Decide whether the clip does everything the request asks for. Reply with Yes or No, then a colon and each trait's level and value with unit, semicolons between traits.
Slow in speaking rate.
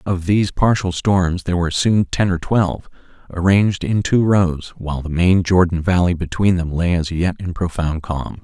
No: average, 190 wpm